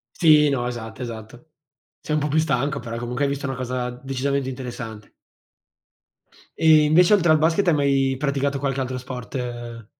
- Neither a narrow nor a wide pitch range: Yes, average, 3.3 semitones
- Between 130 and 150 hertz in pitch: Yes, low, 135 Hz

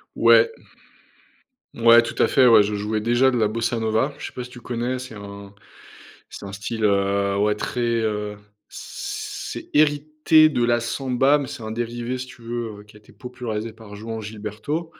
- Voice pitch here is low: Yes, low, 115 Hz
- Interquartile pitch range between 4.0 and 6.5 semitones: No, average, 2.9 semitones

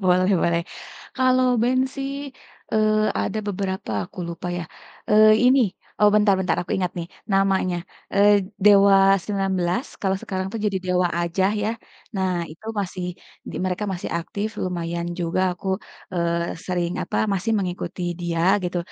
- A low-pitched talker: No, high, 190 Hz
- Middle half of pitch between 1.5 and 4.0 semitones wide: Yes, average, 2.9 semitones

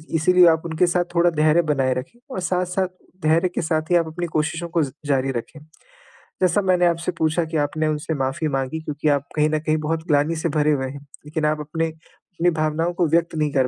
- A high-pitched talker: No, medium, 160 Hz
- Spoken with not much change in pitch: Yes, narrow, 2.1 semitones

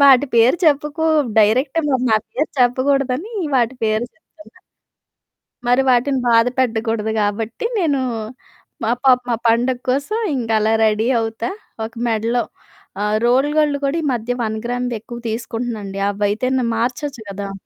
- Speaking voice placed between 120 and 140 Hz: No, high, 245 Hz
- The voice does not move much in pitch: No, average, 3.2 semitones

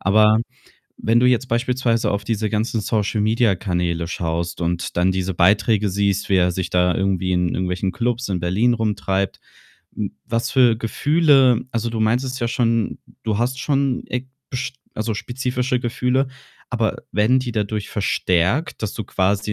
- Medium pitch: No, low, 110 Hz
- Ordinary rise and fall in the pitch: Yes, average, 4.4 semitones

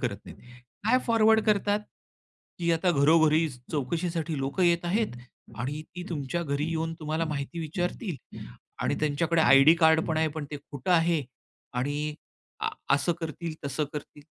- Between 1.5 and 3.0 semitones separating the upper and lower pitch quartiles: Yes, average, 2.7 semitones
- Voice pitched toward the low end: No, medium, 160 Hz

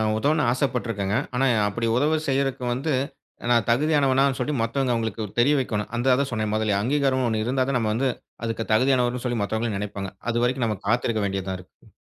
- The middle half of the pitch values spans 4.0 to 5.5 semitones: No, average, 3.5 semitones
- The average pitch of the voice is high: No, low, 120 Hz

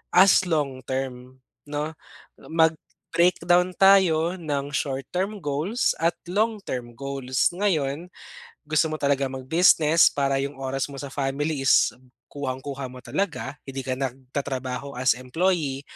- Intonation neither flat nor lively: Yes, average, 4.1 semitones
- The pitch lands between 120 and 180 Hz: Yes, medium, 140 Hz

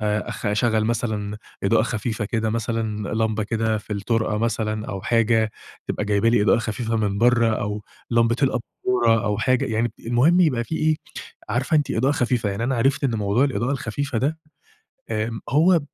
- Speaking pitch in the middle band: No, low, 115 Hz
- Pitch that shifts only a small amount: Yes, narrow, 2.3 semitones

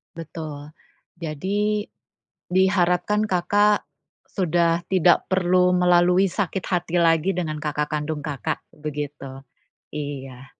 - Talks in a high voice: No, medium, 170 Hz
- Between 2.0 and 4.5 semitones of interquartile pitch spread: Yes, average, 3.8 semitones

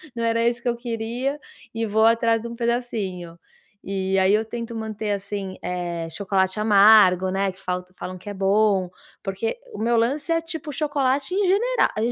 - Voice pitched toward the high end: Yes, high, 220 Hz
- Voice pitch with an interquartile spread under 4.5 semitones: Yes, average, 3.7 semitones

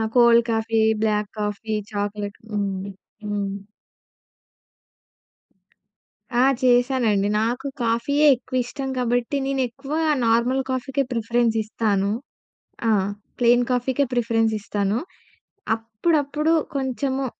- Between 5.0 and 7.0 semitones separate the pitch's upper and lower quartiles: No, average, 3.5 semitones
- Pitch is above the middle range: Yes, high, 235 Hz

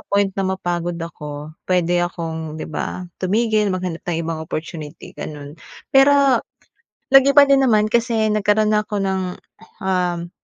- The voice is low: No, medium, 185 Hz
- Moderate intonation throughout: Yes, average, 4.5 semitones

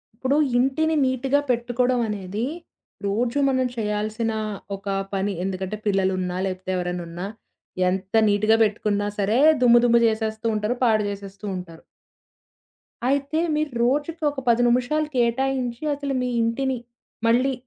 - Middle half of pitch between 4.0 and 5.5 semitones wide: Yes, average, 4.4 semitones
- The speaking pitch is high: Yes, high, 230 Hz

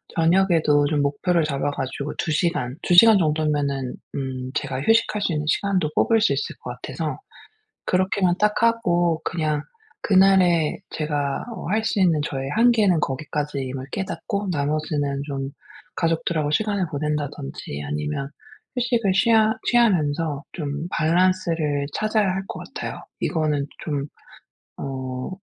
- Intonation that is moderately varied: Yes, average, 5.0 semitones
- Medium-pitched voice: Yes, medium, 155 Hz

